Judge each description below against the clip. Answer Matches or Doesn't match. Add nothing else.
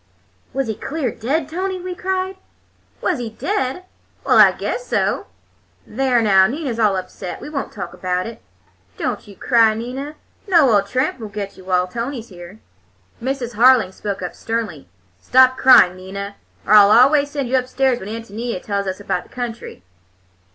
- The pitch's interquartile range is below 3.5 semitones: Doesn't match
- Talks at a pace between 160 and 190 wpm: Matches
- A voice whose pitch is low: Doesn't match